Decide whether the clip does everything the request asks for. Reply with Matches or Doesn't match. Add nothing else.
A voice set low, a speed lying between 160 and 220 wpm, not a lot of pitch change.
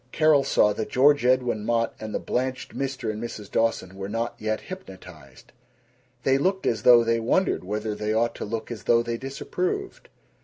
Doesn't match